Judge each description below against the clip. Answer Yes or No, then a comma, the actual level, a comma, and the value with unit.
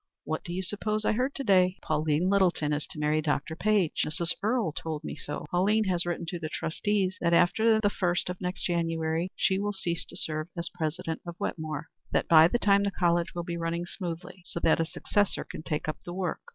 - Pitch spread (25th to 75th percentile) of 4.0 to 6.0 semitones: No, average, 3.1 semitones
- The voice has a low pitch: No, medium, 175 Hz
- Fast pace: Yes, fast, 220 wpm